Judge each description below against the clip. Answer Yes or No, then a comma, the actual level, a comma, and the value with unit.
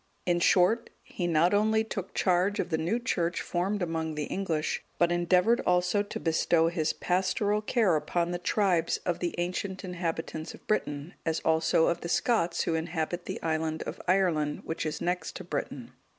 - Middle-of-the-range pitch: Yes, medium, 175 Hz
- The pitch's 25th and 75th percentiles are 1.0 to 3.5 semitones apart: Yes, average, 2.7 semitones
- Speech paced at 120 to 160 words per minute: No, average, 180 wpm